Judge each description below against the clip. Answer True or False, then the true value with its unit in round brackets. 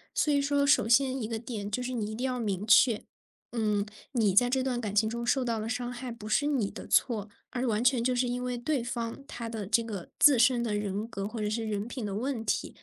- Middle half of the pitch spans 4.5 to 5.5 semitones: False (2.8 semitones)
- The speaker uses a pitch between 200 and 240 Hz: True (235 Hz)